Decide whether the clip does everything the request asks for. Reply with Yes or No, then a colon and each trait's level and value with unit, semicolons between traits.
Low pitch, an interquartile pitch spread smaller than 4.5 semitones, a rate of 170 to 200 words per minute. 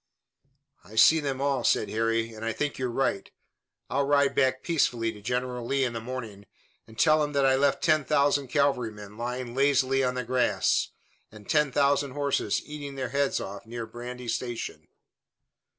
Yes: low, 130 Hz; average, 3.5 semitones; average, 175 wpm